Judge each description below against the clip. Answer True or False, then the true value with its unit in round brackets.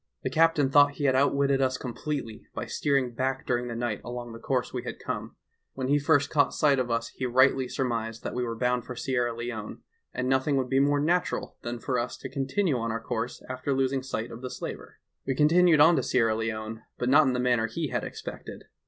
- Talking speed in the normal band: False (230 wpm)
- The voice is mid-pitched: False (130 Hz)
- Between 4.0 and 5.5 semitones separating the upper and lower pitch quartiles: False (2.6 semitones)